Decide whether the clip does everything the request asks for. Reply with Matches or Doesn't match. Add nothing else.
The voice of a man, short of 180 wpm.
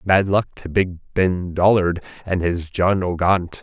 Matches